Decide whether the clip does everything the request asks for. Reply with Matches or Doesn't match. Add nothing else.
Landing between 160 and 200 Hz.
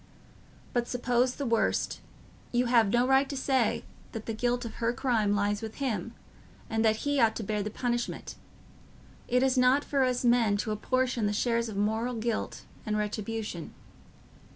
Doesn't match